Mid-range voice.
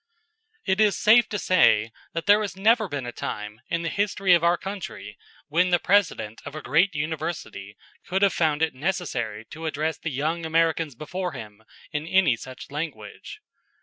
Yes: medium, 165 Hz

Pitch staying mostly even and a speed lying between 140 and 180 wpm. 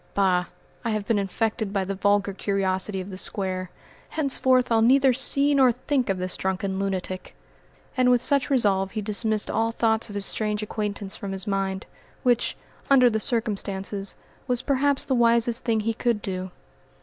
No: average, 3.8 semitones; average, 175 wpm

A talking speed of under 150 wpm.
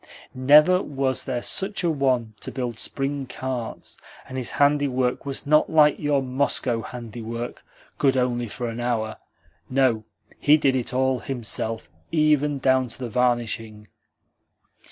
Yes: average, 140 wpm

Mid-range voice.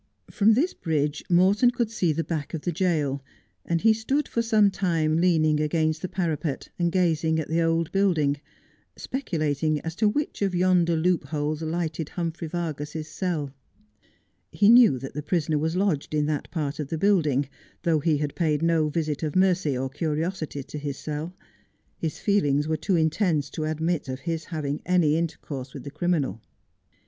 Yes: medium, 160 Hz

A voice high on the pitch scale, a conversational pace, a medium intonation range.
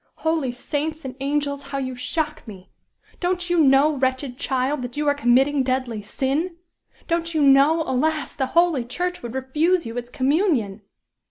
Yes: very high, 280 Hz; average, 165 wpm; average, 3.6 semitones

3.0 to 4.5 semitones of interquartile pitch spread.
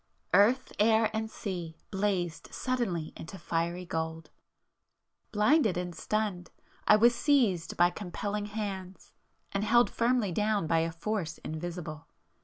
Yes: average, 4.2 semitones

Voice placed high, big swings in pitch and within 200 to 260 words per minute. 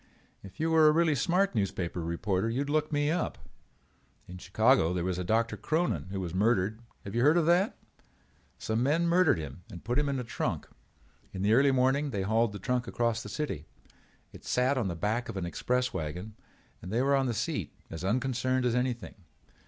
No: low, 120 Hz; wide, 6.5 semitones; fast, 205 wpm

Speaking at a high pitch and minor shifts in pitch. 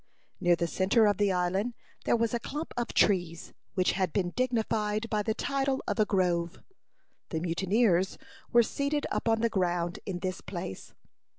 No: high, 200 Hz; average, 4.6 semitones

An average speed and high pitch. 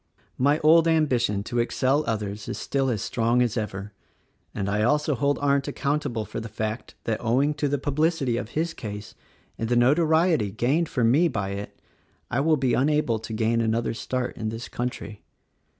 No: average, 180 wpm; low, 120 Hz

